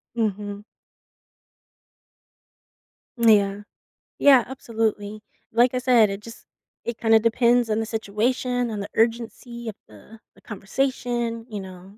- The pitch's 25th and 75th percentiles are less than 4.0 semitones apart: Yes, narrow, 2.4 semitones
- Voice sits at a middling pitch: No, high, 225 Hz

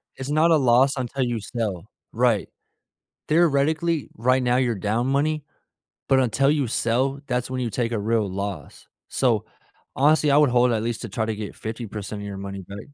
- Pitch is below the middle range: Yes, low, 120 Hz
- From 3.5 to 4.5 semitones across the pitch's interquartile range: Yes, average, 4.0 semitones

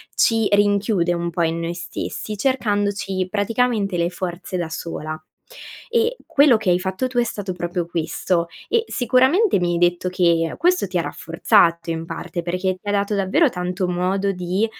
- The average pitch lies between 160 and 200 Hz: Yes, medium, 185 Hz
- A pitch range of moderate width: Yes, average, 3.5 semitones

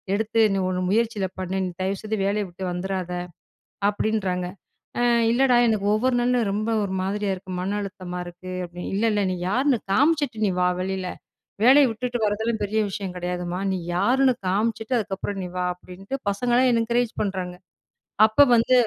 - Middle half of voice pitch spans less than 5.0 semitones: Yes, average, 3.7 semitones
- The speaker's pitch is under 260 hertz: Yes, high, 205 Hz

